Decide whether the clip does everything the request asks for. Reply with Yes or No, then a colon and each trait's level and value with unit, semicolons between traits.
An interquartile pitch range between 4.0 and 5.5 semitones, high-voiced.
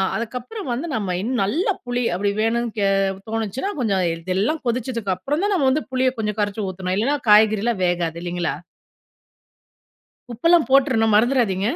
Yes: average, 4.7 semitones; high, 225 Hz